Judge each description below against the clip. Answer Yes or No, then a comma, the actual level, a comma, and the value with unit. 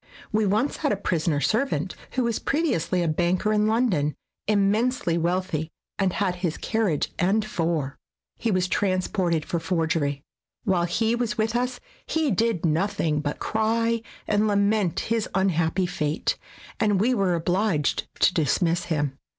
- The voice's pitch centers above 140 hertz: Yes, medium, 185 Hz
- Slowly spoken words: No, average, 150 wpm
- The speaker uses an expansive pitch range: No, average, 4.7 semitones